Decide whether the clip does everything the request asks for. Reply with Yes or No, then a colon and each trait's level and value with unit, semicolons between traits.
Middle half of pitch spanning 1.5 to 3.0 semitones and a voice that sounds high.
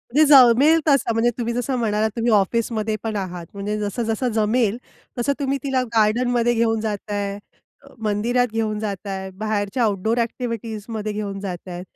Yes: average, 2.7 semitones; high, 220 Hz